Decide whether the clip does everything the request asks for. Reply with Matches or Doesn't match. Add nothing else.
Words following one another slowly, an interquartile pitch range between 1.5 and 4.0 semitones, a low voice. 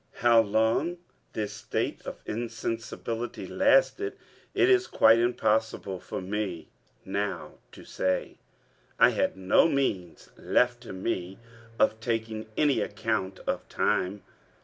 Matches